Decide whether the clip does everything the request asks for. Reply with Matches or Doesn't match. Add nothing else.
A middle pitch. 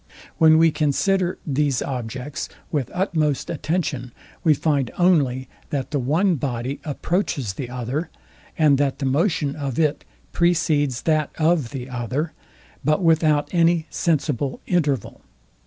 Matches